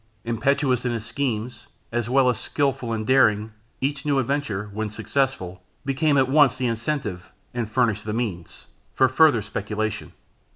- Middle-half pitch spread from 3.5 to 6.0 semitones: Yes, average, 3.9 semitones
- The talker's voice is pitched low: Yes, low, 120 Hz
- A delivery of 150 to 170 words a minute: Yes, average, 155 wpm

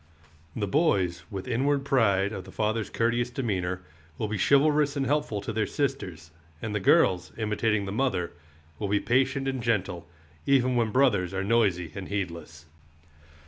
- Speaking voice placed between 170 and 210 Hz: No, low, 110 Hz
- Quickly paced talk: No, average, 160 wpm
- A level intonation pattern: No, average, 5.3 semitones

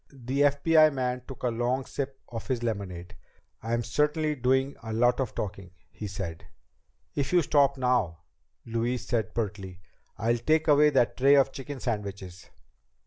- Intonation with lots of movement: No, average, 4.4 semitones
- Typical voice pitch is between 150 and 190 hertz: No, low, 125 Hz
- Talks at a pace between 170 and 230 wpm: No, average, 155 wpm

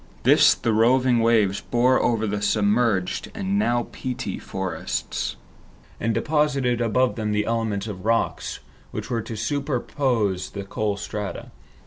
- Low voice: Yes, low, 115 Hz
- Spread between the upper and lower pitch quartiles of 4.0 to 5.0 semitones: No, average, 3.3 semitones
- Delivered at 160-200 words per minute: No, slow, 135 wpm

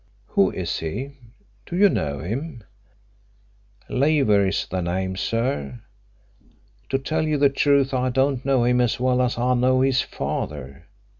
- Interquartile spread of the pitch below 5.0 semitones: No, wide, 5.5 semitones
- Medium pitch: No, low, 125 Hz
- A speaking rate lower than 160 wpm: Yes, average, 150 wpm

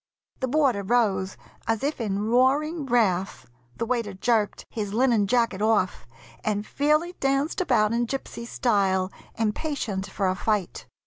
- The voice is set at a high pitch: Yes, high, 225 Hz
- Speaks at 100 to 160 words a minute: Yes, average, 140 wpm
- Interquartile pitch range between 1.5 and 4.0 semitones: No, average, 4.5 semitones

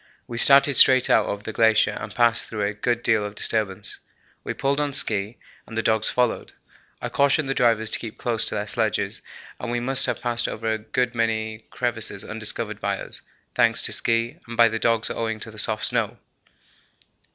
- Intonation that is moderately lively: No, narrow, 1.9 semitones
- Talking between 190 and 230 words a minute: Yes, average, 200 wpm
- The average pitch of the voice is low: Yes, low, 115 Hz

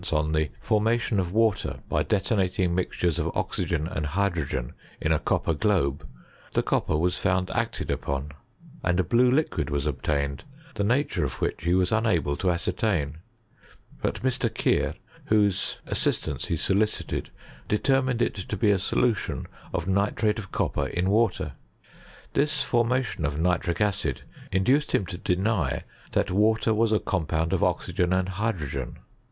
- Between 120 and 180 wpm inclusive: Yes, average, 150 wpm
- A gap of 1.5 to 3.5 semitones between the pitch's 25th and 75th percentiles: No, average, 4.8 semitones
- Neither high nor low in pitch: No, very low, 95 Hz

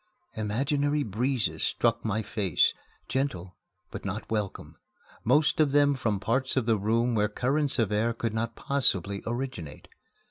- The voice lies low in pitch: Yes, low, 115 Hz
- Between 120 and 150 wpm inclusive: Yes, average, 145 wpm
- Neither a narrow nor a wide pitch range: Yes, average, 4.3 semitones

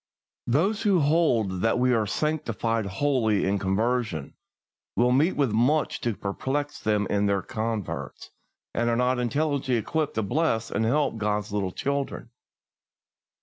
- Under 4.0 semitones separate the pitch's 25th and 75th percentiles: No, average, 5.3 semitones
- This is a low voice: Yes, low, 120 Hz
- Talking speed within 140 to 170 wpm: Yes, average, 145 wpm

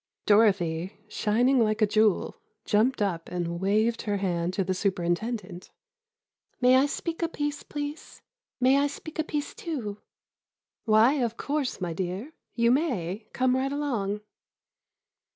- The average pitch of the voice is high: Yes, high, 220 Hz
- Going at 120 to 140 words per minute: Yes, slow, 135 wpm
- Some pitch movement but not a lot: No, wide, 5.9 semitones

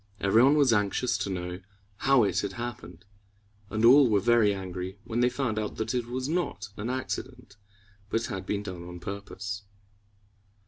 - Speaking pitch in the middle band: No, low, 105 Hz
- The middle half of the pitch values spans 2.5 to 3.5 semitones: No, average, 4.0 semitones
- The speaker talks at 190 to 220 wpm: No, average, 175 wpm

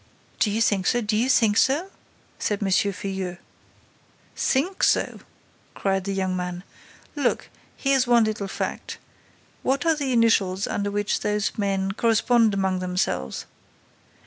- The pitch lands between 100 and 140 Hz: No, high, 205 Hz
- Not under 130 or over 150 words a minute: Yes, average, 140 wpm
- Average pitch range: Yes, average, 3.8 semitones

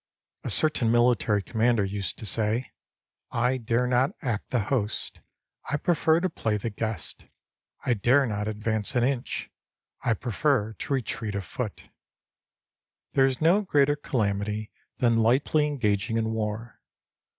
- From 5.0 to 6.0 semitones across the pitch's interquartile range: No, average, 3.8 semitones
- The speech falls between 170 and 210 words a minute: No, average, 145 wpm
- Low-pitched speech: Yes, low, 115 Hz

